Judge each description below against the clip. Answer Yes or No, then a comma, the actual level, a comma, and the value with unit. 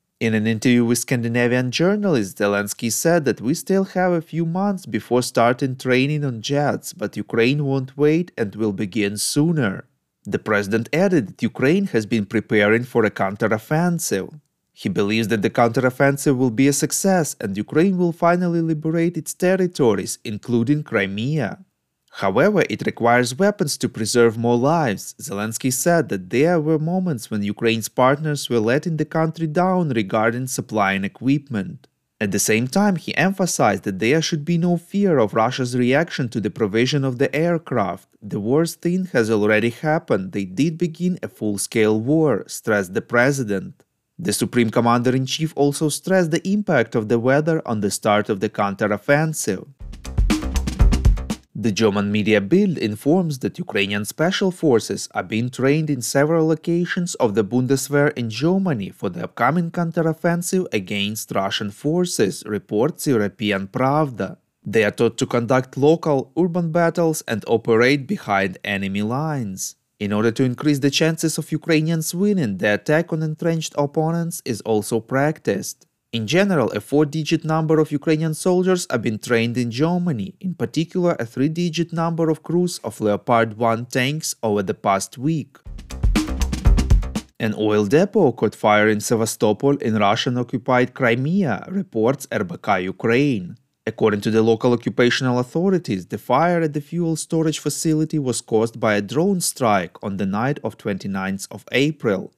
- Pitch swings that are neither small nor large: No, wide, 6.5 semitones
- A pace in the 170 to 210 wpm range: No, average, 155 wpm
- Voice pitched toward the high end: No, low, 135 Hz